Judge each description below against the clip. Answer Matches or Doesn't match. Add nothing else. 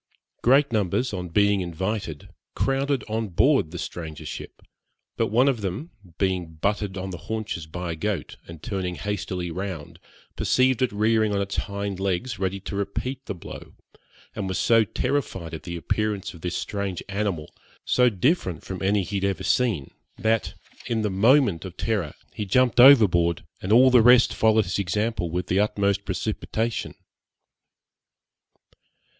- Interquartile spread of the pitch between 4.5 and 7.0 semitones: Doesn't match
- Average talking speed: Matches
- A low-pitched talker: Matches